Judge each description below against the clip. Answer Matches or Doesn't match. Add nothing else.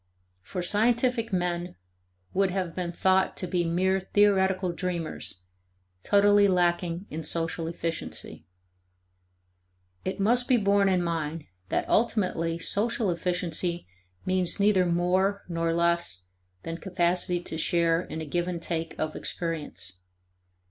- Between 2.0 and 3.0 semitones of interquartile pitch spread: Matches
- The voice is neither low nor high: Matches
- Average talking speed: Doesn't match